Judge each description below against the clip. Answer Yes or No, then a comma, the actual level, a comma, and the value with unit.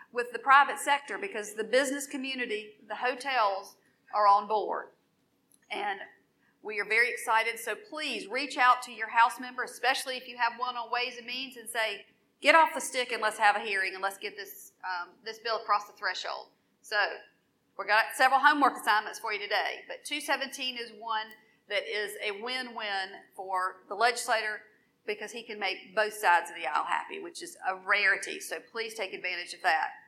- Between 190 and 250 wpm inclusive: Yes, average, 195 wpm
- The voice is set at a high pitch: Yes, high, 225 Hz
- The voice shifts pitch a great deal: No, average, 3.8 semitones